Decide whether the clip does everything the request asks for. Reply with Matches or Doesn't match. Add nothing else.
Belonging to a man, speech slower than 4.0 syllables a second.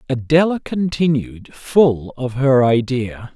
Matches